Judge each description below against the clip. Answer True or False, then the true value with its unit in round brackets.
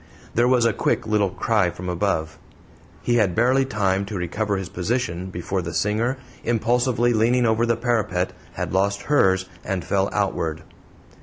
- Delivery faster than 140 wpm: True (160 wpm)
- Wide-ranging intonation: False (4.2 semitones)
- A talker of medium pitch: False (105 Hz)